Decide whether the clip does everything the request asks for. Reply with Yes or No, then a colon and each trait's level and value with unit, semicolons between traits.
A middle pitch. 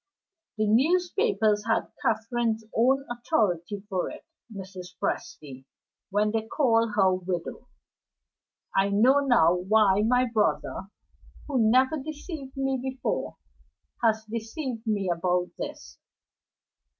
No: high, 220 Hz